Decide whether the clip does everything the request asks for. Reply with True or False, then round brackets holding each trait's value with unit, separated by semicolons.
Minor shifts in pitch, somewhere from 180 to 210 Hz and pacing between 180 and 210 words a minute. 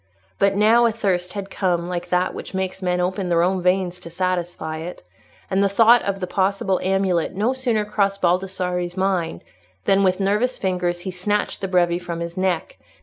True (1.9 semitones; 185 Hz; 190 wpm)